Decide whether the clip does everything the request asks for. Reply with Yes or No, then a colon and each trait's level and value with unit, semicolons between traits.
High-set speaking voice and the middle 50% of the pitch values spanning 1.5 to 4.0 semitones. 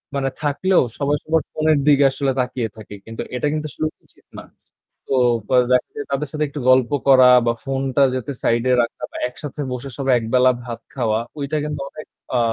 No: low, 135 Hz; average, 2.8 semitones